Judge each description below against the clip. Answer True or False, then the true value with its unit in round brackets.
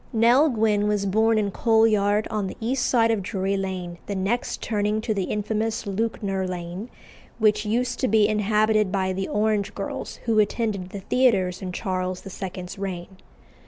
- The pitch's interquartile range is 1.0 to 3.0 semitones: True (2.5 semitones)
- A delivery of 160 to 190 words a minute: True (170 wpm)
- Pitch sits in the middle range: False (210 Hz)